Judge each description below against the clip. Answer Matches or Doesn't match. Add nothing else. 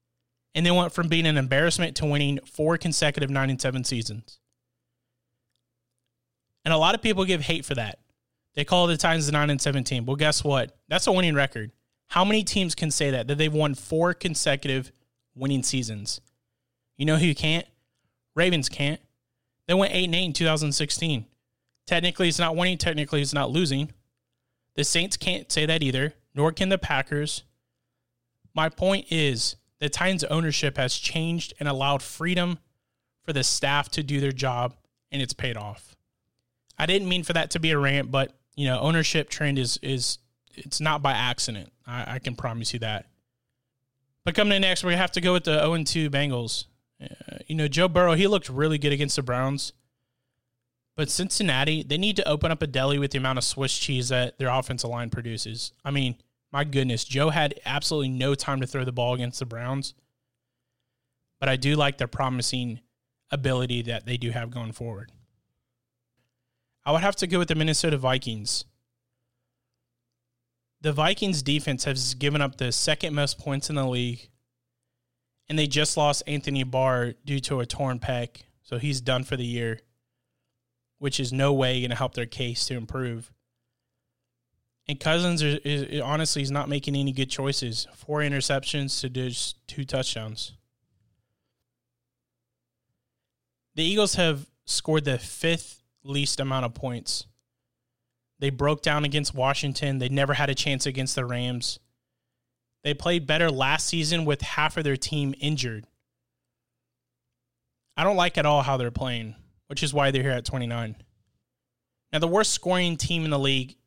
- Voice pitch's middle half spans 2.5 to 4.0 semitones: Matches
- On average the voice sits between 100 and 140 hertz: Matches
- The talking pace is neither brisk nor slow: Matches